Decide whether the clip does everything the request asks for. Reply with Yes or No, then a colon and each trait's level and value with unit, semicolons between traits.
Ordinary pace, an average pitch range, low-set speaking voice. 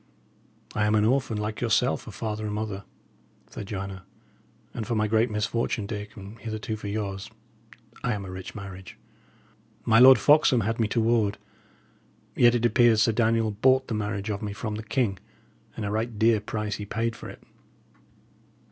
No: average, 180 wpm; narrow, 1.9 semitones; low, 110 Hz